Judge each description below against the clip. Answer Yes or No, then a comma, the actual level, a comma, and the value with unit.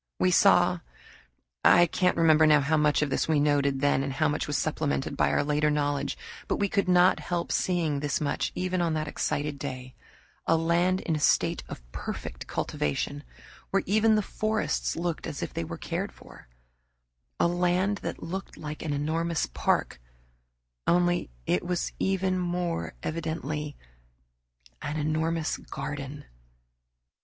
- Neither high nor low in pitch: Yes, medium, 160 Hz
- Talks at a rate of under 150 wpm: No, average, 155 wpm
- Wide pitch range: No, average, 3.2 semitones